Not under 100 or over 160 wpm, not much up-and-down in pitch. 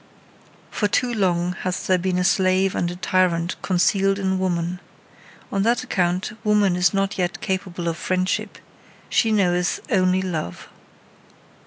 Yes: average, 145 wpm; narrow, 1.7 semitones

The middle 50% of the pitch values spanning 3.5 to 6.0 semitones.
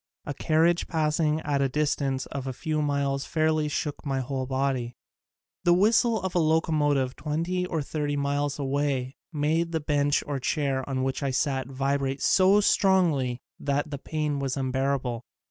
No: narrow, 2.5 semitones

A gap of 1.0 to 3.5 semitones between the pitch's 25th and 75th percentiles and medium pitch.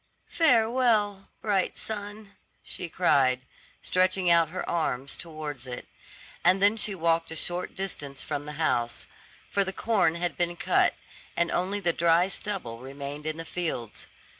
No: average, 4.7 semitones; medium, 175 Hz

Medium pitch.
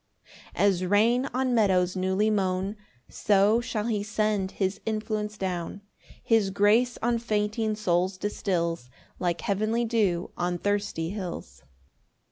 No: high, 205 Hz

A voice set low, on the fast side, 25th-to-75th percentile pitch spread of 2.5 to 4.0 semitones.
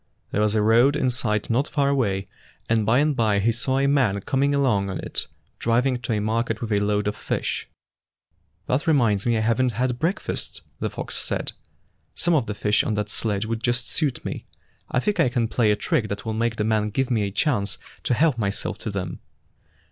Yes: low, 115 Hz; fast, 225 wpm; average, 3.7 semitones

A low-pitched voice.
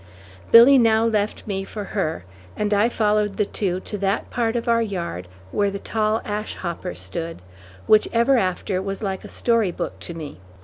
No: high, 205 Hz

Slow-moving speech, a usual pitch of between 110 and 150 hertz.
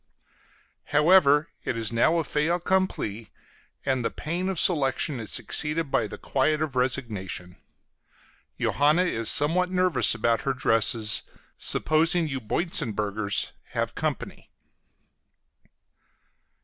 Yes: slow, 110 wpm; medium, 140 Hz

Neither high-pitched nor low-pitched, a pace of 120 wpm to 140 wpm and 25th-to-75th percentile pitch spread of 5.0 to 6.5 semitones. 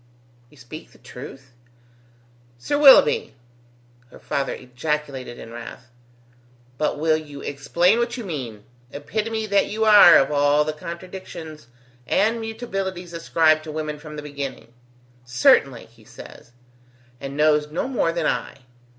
Yes: medium, 155 Hz; slow, 135 wpm; wide, 5.5 semitones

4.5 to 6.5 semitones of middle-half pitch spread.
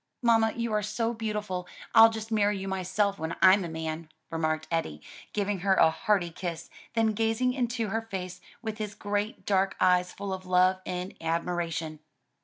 No: average, 3.8 semitones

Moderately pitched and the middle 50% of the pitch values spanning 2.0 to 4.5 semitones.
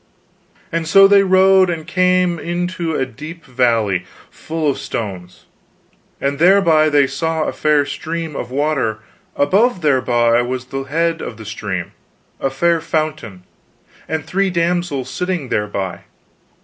No: medium, 155 Hz; average, 5.2 semitones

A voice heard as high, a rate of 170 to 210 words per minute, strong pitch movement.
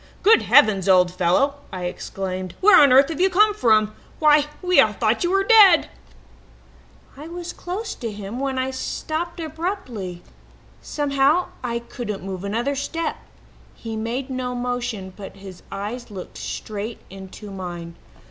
No: high, 245 Hz; average, 155 wpm; wide, 7.9 semitones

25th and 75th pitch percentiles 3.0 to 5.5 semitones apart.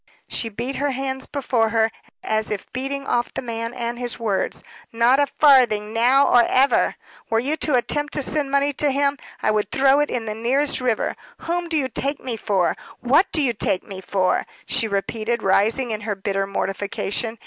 Yes: average, 4.1 semitones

